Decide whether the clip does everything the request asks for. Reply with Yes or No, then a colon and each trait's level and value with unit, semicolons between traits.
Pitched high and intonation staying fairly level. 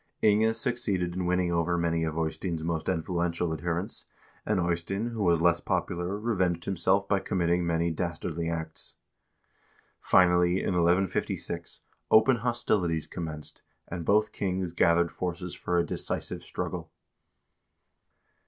No: very low, 85 Hz; narrow, 2.1 semitones